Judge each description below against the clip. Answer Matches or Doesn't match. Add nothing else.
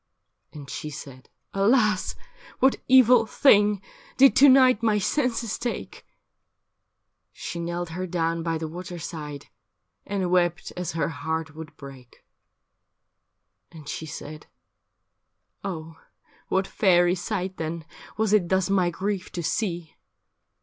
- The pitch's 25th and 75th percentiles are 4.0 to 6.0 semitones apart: Matches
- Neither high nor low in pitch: Matches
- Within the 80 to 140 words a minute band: Matches